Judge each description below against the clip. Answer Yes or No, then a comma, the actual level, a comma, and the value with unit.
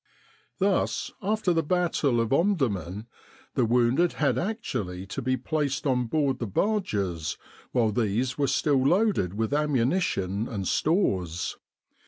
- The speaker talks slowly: Yes, slow, 130 wpm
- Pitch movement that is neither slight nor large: No, wide, 7.4 semitones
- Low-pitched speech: Yes, low, 130 Hz